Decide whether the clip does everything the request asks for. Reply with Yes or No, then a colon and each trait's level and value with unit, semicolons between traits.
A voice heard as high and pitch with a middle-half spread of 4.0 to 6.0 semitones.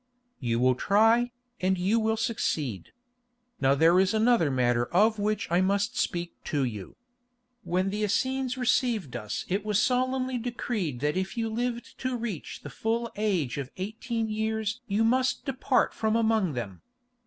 Yes: high, 210 Hz; wide, 5.5 semitones